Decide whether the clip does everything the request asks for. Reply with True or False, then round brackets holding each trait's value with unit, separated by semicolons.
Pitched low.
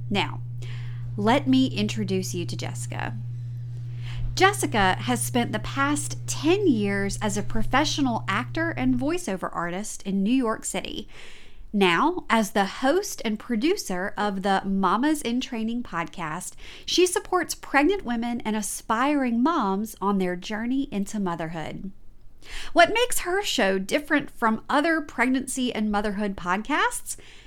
False (200 Hz)